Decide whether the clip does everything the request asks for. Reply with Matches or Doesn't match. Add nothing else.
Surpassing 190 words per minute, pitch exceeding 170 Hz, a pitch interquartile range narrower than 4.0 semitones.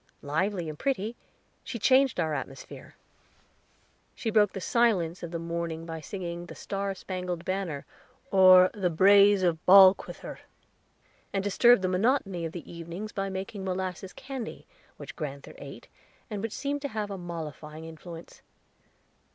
Doesn't match